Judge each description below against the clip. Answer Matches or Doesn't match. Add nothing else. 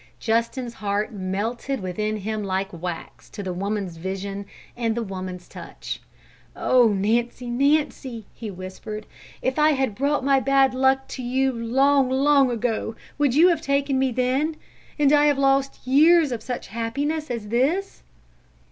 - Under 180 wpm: Matches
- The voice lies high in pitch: Matches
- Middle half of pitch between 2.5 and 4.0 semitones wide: Doesn't match